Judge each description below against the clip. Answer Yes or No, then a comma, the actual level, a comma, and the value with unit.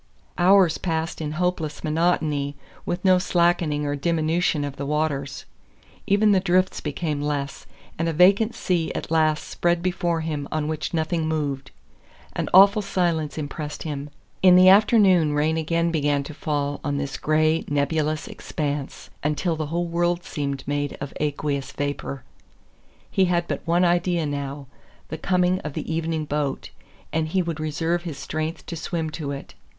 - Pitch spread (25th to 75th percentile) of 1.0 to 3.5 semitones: Yes, average, 2.9 semitones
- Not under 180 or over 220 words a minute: No, average, 160 wpm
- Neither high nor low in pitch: Yes, medium, 160 Hz